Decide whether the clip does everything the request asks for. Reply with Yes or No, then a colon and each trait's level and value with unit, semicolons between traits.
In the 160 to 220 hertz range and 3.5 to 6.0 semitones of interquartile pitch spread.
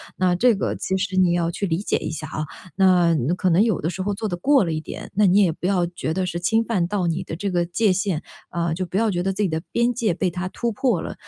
No: medium, 185 Hz; average, 3.0 semitones